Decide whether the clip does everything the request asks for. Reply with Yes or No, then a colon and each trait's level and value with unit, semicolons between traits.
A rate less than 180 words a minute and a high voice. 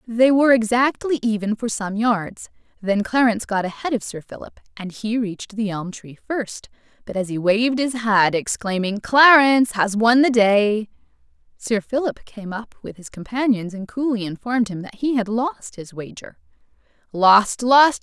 Yes: average, 170 wpm; high, 225 Hz